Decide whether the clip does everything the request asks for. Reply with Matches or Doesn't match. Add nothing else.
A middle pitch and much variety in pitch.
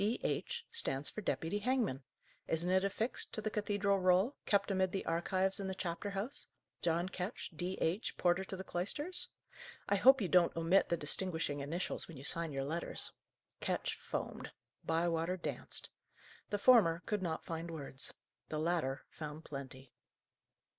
Doesn't match